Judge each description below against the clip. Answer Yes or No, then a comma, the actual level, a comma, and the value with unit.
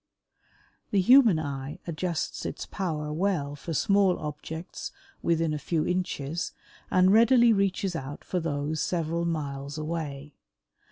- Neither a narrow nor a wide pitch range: Yes, average, 3.7 semitones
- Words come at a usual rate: No, slow, 125 wpm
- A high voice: No, medium, 165 Hz